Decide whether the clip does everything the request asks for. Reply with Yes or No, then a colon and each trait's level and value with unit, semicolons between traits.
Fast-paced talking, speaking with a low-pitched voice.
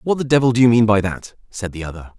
Yes: fast, 300 wpm; low, 110 Hz